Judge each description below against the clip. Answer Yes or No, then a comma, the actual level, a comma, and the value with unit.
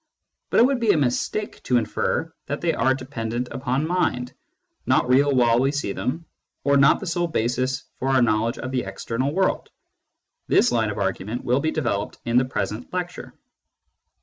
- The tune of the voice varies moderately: Yes, average, 3.5 semitones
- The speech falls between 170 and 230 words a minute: Yes, average, 180 wpm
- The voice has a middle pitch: No, low, 130 Hz